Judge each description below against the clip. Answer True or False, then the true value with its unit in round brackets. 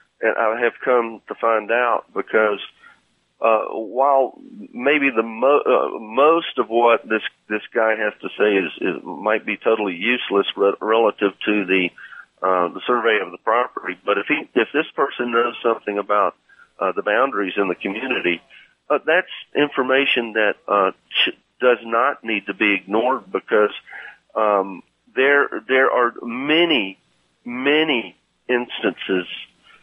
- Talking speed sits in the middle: True (150 wpm)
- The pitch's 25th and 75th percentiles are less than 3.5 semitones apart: False (3.8 semitones)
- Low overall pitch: True (115 Hz)